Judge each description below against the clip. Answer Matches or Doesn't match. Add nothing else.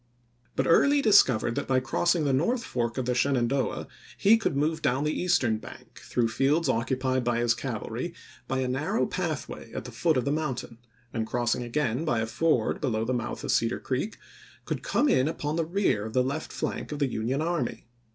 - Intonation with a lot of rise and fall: Doesn't match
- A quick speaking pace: Matches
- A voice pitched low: Matches